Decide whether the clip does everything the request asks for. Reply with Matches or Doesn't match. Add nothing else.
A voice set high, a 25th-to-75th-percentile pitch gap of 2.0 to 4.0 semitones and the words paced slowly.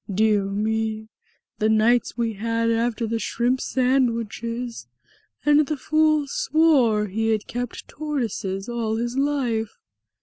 Matches